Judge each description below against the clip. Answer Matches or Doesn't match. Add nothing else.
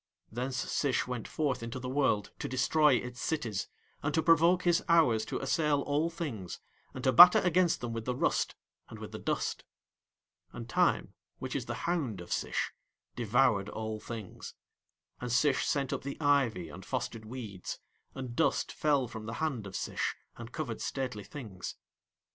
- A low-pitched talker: Matches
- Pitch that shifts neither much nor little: Matches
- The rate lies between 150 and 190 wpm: Matches